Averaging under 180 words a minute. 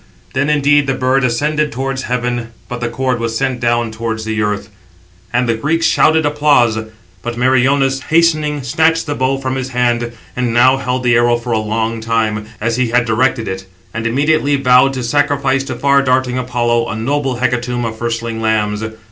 No: average, 185 wpm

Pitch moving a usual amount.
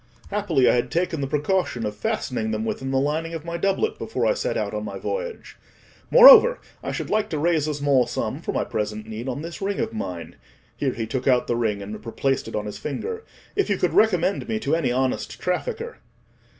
No: wide, 8.6 semitones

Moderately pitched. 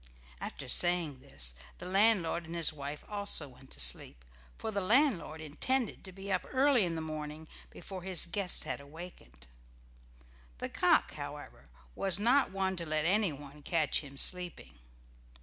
Yes: medium, 170 Hz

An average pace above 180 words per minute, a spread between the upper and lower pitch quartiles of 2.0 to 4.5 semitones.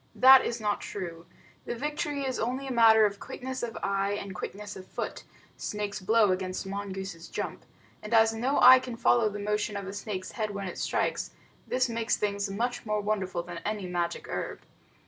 Yes: average, 190 wpm; average, 3.1 semitones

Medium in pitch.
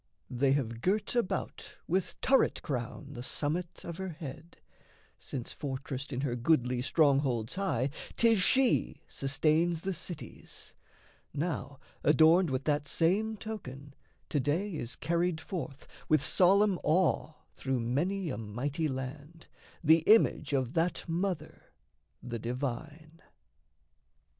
Yes: medium, 155 Hz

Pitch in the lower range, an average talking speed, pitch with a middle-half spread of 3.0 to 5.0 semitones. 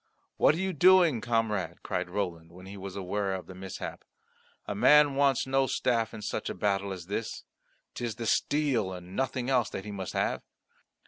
No: low, 105 Hz; average, 190 wpm; wide, 5.6 semitones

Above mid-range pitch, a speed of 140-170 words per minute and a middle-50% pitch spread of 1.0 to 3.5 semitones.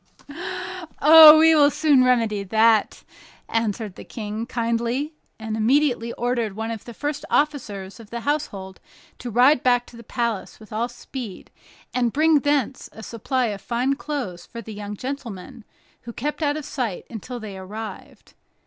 No: high, 235 Hz; average, 160 wpm; average, 4.3 semitones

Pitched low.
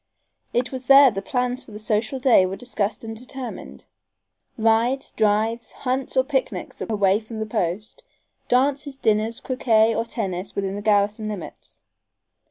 No: high, 225 Hz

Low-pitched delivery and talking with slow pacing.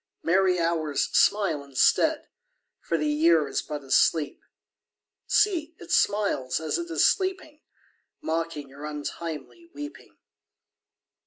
No: medium, 165 Hz; slow, 115 wpm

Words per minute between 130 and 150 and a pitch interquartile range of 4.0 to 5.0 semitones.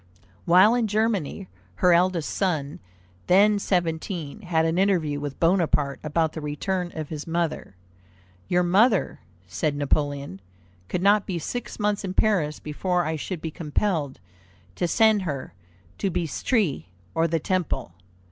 Yes: average, 145 wpm; average, 4.3 semitones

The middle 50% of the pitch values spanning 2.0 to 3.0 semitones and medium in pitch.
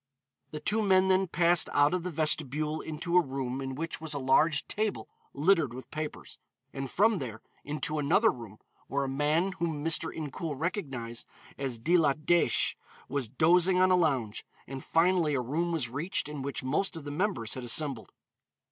No: average, 4.3 semitones; medium, 150 Hz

